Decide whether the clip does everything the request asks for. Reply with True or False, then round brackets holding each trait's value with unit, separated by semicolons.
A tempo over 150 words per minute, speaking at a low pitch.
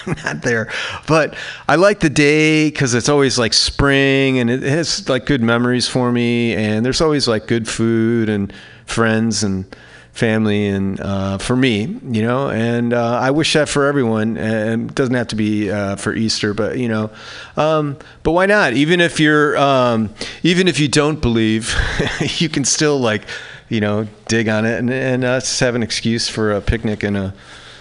True (190 wpm; 120 Hz)